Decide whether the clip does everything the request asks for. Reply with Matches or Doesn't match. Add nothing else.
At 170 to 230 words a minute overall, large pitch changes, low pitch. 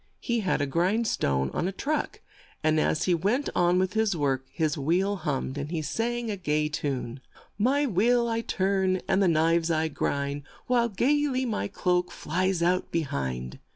Doesn't match